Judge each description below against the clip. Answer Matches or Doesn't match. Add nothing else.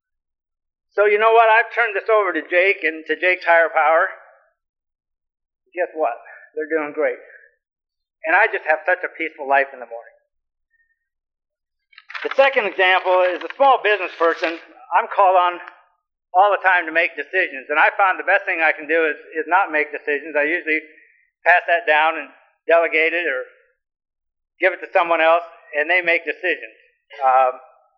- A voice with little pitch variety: Doesn't match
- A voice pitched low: Doesn't match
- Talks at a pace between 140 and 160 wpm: Doesn't match